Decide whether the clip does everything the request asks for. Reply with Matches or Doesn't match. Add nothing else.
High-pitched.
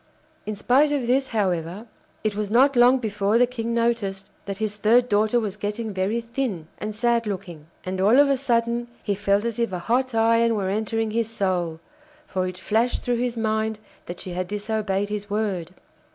Matches